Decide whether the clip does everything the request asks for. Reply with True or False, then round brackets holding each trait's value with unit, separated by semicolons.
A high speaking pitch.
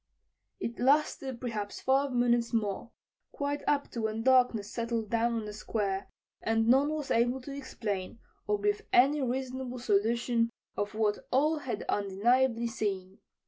True (235 Hz)